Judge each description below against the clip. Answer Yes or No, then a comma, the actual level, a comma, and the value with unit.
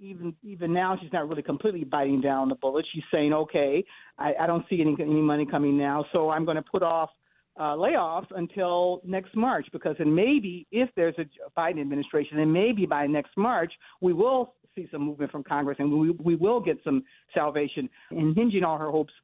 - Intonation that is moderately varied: Yes, average, 4.0 semitones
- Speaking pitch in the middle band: Yes, medium, 165 Hz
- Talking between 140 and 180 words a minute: No, fast, 205 wpm